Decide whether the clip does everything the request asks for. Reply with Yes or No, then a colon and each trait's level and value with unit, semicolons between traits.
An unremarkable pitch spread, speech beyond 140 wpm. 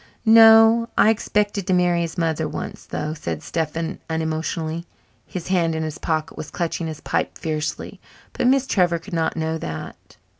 Yes: average, 3.2 semitones; average, 165 wpm